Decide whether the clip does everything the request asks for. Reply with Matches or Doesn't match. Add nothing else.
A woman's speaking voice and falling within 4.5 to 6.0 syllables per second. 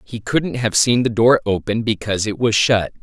Doesn't match